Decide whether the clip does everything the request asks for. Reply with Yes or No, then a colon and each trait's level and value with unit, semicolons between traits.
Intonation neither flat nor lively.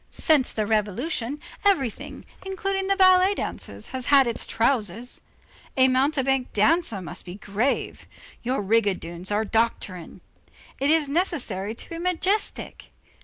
No: wide, 7.5 semitones